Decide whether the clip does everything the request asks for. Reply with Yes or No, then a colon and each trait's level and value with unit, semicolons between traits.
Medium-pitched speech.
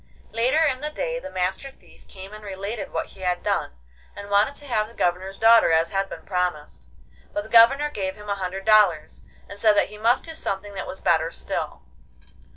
No: high, 205 Hz